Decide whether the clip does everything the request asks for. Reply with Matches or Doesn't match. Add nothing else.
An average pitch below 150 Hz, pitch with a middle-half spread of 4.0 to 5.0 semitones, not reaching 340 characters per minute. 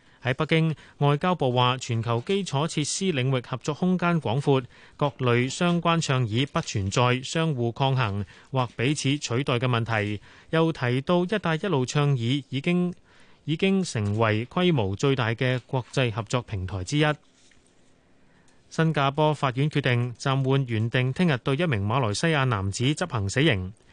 Matches